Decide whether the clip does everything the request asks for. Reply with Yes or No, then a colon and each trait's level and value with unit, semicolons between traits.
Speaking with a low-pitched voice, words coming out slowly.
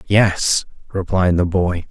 Yes: very low, 90 Hz; slow, 125 wpm